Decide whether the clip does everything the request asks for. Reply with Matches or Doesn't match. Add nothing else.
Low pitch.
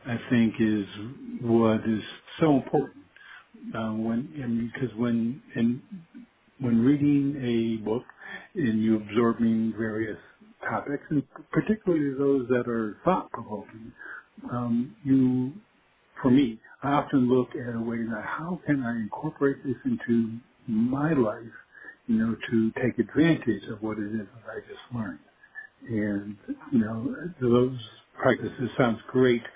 Matches